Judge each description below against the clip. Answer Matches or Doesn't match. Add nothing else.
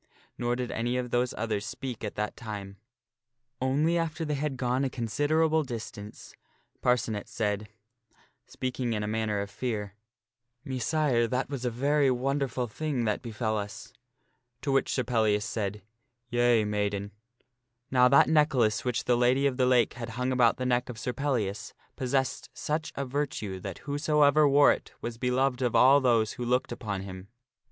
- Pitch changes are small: Doesn't match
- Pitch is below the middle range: Matches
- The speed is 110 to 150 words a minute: Doesn't match